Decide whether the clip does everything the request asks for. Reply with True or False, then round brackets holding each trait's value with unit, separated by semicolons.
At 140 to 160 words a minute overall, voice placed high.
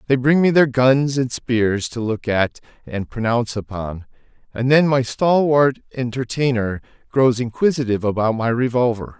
False (150 wpm; 125 Hz)